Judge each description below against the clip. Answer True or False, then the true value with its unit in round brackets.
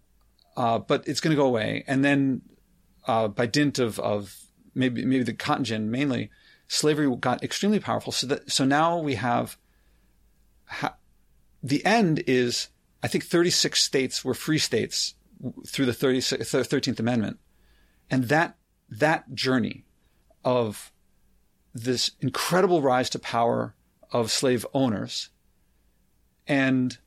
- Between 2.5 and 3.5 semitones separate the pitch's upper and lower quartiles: True (3.2 semitones)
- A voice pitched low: True (130 Hz)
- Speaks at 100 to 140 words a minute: True (135 wpm)